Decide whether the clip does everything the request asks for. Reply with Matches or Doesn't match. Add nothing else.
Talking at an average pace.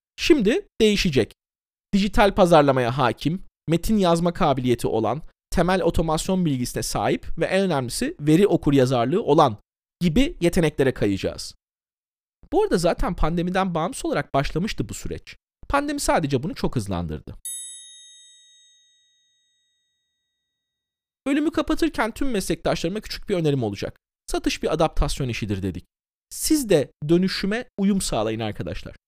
Matches